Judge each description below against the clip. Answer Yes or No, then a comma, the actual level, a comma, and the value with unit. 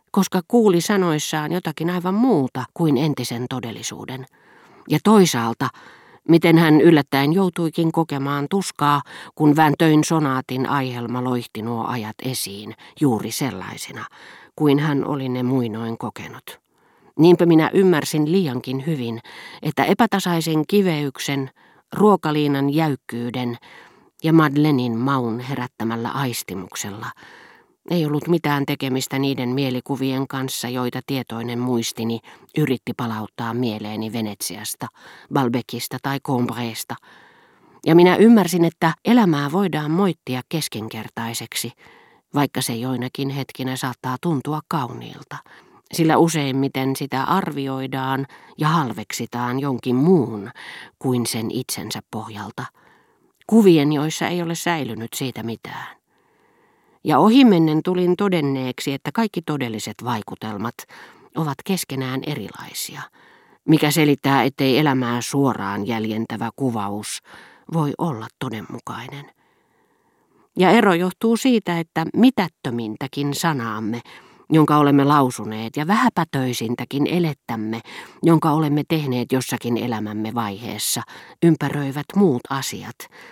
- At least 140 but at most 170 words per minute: No, average, 100 wpm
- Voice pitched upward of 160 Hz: No, medium, 140 Hz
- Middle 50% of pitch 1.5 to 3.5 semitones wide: No, average, 5.0 semitones